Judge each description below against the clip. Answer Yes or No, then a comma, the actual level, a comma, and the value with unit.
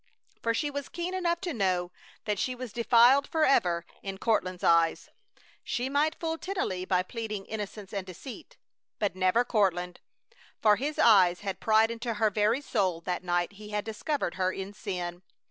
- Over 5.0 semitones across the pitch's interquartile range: Yes, wide, 5.5 semitones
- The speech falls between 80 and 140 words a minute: No, average, 170 wpm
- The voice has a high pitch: Yes, high, 210 Hz